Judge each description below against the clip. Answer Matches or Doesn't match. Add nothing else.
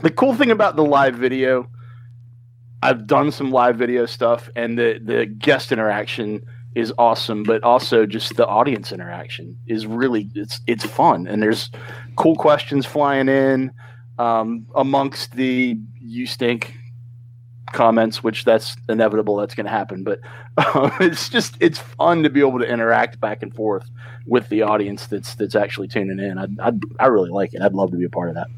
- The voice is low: Matches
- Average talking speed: Matches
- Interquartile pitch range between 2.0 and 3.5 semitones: Matches